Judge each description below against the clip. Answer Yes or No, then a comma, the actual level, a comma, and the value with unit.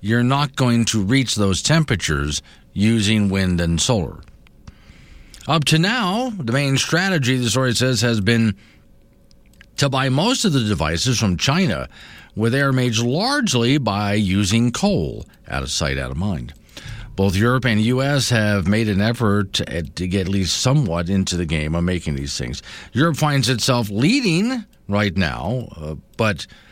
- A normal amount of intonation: No, wide, 5.9 semitones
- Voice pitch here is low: Yes, low, 110 Hz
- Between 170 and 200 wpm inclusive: No, average, 160 wpm